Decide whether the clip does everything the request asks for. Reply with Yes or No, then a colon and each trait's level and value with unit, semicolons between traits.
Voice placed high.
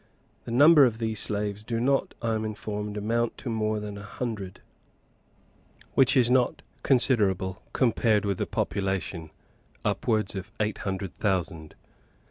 No: low, 105 Hz